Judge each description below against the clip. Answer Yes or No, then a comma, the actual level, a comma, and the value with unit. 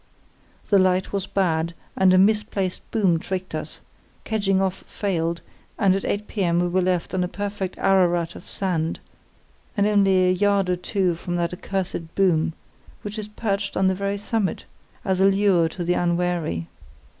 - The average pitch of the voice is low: No, medium, 185 Hz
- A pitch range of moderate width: No, narrow, 2.1 semitones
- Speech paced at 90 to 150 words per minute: No, average, 170 wpm